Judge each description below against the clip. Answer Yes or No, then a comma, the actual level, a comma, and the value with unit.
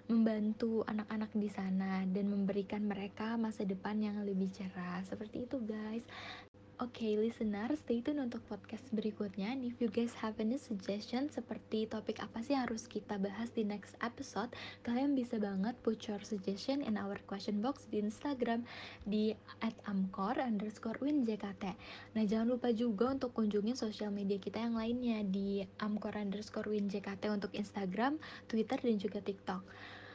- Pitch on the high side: Yes, high, 215 Hz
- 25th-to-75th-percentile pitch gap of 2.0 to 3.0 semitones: Yes, narrow, 2.4 semitones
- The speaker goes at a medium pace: No, fast, 155 wpm